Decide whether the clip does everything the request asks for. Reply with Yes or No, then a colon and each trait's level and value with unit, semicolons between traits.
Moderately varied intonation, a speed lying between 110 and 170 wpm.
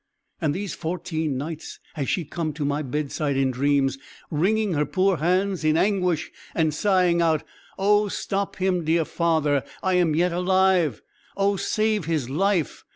Yes: average, 4.0 semitones; average, 160 wpm